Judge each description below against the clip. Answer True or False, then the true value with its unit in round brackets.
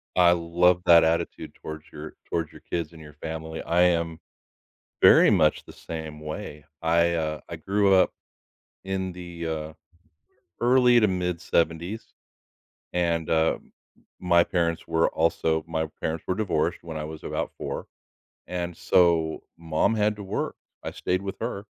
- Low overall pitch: True (85 Hz)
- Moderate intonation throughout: False (2.1 semitones)